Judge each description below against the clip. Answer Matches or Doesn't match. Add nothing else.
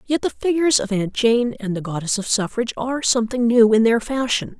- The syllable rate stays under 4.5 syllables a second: Doesn't match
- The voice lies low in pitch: Doesn't match